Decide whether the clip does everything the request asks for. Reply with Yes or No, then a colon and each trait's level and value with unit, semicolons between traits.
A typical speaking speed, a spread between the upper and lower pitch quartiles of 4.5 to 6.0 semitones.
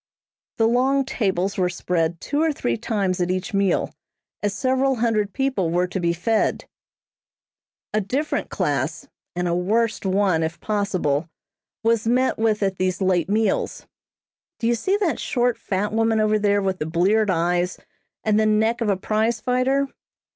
No: average, 165 wpm; average, 4.0 semitones